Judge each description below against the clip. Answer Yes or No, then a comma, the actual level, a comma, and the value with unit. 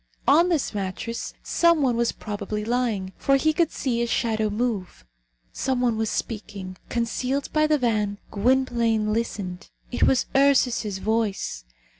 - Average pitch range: Yes, average, 3.8 semitones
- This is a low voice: No, high, 230 Hz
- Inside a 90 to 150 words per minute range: Yes, average, 145 wpm